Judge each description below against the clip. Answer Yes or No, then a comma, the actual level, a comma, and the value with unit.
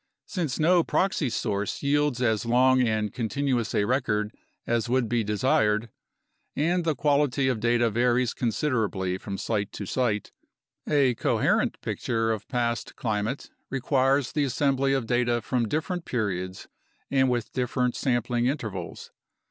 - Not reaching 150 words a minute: Yes, average, 140 wpm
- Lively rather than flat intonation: No, average, 3.7 semitones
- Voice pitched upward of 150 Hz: No, low, 120 Hz